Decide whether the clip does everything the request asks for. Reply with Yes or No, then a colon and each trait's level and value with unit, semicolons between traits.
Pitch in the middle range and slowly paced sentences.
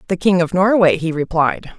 No: medium, 175 Hz; average, 200 wpm